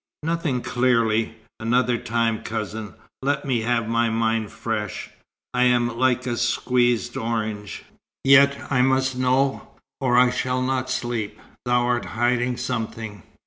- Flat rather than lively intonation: Yes, narrow, 2.0 semitones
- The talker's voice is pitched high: No, low, 120 Hz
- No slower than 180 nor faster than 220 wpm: No, slow, 135 wpm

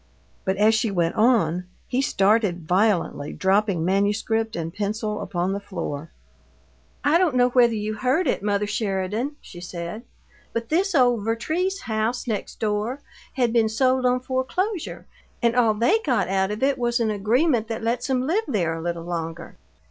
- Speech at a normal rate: Yes, average, 170 wpm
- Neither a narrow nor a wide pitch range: Yes, average, 4.4 semitones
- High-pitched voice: Yes, high, 220 Hz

